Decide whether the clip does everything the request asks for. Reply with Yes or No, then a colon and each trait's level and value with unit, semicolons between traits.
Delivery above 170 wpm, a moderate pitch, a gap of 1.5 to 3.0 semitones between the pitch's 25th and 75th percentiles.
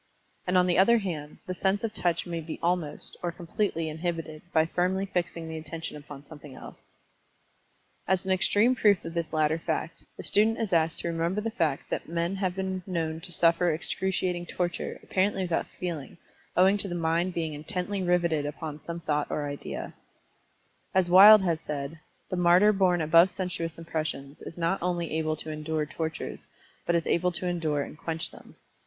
Yes: average, 185 wpm; medium, 170 Hz; narrow, 2.5 semitones